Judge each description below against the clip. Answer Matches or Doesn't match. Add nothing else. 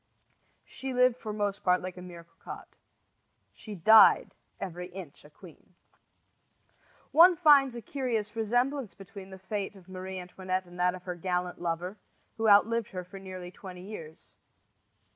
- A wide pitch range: Doesn't match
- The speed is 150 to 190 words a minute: Matches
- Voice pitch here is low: Doesn't match